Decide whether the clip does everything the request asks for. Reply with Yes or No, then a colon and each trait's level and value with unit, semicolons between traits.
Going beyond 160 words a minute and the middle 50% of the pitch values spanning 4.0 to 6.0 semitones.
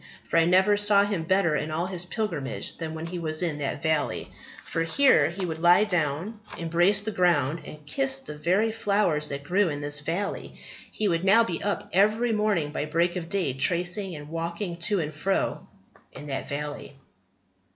Yes: average, 190 wpm; average, 4.6 semitones